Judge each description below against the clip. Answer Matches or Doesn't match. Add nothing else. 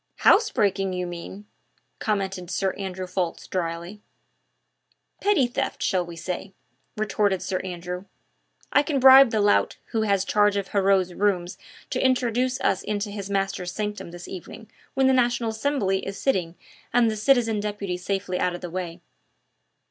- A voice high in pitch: Matches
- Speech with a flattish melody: Doesn't match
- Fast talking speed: Doesn't match